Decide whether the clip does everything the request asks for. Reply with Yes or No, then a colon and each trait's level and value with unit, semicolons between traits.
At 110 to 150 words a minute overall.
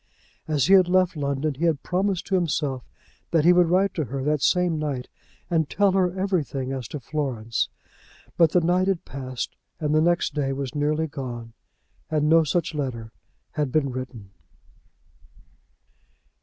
No: average, 165 wpm